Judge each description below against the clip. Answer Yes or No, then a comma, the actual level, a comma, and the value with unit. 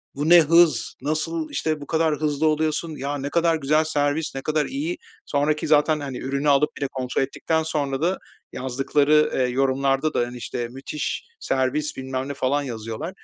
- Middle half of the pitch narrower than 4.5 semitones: Yes, narrow, 2.6 semitones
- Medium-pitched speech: Yes, medium, 145 Hz